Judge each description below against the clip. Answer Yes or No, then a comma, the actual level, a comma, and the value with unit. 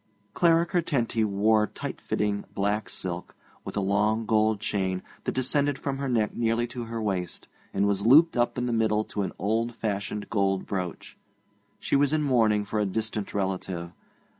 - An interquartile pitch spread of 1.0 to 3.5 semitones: Yes, average, 3.2 semitones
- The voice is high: No, low, 110 Hz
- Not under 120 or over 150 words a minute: No, average, 175 wpm